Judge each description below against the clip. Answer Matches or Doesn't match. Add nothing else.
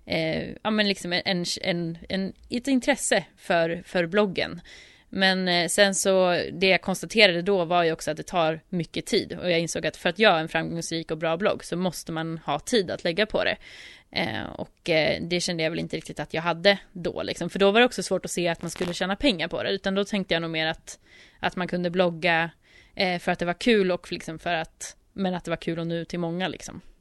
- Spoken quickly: Matches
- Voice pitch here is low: Doesn't match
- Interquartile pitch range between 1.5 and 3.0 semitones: Matches